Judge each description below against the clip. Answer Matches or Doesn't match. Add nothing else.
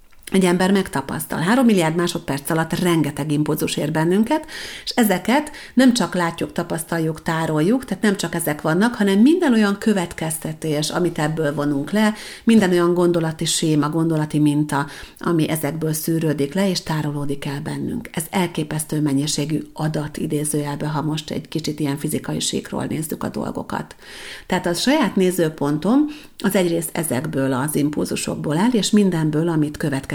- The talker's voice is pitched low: Doesn't match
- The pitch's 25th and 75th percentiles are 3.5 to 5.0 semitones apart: Matches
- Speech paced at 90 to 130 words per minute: Doesn't match